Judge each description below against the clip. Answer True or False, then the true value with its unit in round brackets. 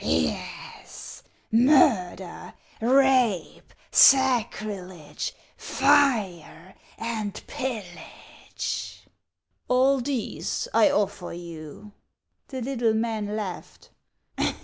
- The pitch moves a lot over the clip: True (6.1 semitones)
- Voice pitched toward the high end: True (220 Hz)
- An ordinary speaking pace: False (80 wpm)